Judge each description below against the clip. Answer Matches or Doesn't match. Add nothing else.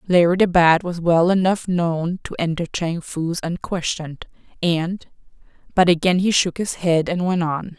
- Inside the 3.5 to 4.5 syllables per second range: Matches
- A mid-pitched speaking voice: Matches